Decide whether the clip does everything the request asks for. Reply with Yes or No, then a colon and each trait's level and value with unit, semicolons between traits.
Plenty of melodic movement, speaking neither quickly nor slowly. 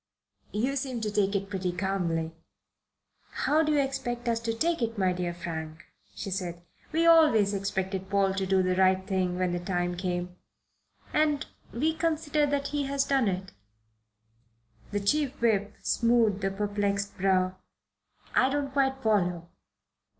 Yes: wide, 6.4 semitones; average, 155 wpm